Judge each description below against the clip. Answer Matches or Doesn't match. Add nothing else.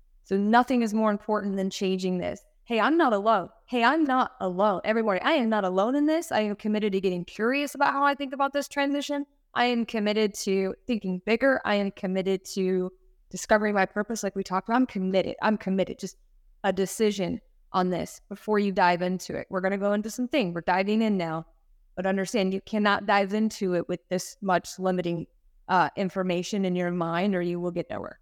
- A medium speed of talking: Doesn't match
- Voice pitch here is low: Doesn't match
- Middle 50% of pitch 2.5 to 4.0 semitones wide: Matches